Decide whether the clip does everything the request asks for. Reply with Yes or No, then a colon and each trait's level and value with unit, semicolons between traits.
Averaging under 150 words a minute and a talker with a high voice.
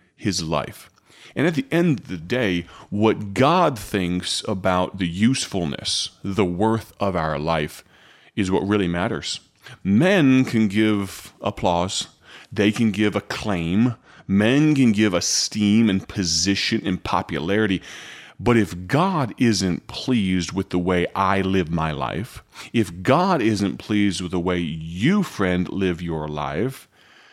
No: average, 140 wpm; low, 100 Hz